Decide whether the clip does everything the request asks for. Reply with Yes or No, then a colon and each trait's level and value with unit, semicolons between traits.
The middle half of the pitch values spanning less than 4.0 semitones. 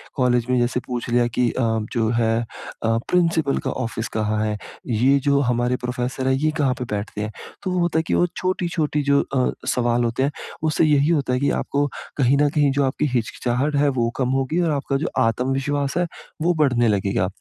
Yes: average, 3.3 semitones